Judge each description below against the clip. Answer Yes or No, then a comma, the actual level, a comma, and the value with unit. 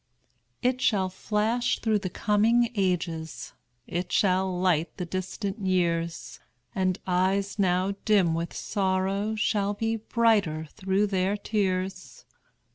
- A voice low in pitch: No, high, 190 Hz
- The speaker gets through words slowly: Yes, slow, 115 wpm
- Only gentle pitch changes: Yes, narrow, 2.3 semitones